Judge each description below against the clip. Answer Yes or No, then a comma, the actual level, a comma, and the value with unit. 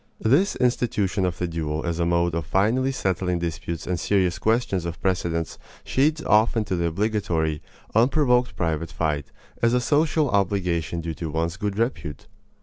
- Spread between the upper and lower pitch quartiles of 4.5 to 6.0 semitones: Yes, wide, 5.4 semitones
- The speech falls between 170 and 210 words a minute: No, average, 160 wpm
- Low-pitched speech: Yes, very low, 90 Hz